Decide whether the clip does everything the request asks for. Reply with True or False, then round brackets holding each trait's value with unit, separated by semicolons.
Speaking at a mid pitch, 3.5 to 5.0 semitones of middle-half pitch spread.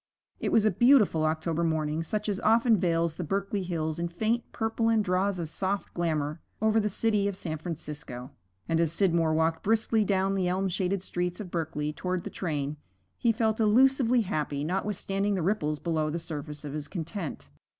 True (180 Hz; 4.7 semitones)